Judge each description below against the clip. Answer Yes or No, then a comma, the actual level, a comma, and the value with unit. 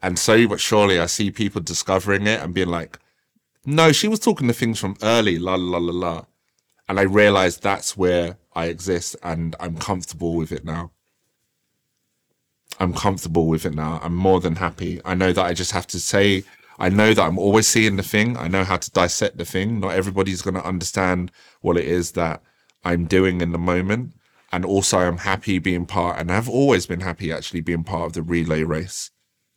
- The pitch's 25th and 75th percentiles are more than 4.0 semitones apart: No, average, 2.7 semitones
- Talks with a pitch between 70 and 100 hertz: Yes, very low, 90 Hz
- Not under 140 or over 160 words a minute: No, fast, 205 wpm